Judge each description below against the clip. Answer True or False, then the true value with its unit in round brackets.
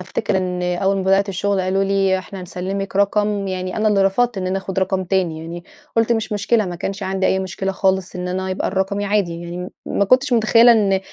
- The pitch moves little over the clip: True (1.5 semitones)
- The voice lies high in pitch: True (195 Hz)